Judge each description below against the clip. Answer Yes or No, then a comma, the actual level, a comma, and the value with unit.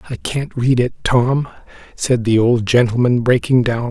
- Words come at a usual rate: Yes, average, 170 wpm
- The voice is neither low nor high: No, low, 120 Hz